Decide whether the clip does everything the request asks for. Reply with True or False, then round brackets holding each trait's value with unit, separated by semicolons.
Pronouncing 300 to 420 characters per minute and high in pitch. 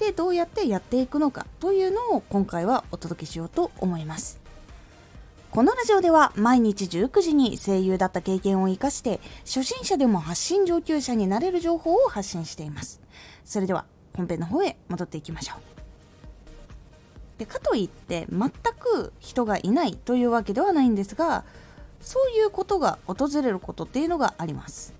True (350 characters per minute; 245 Hz)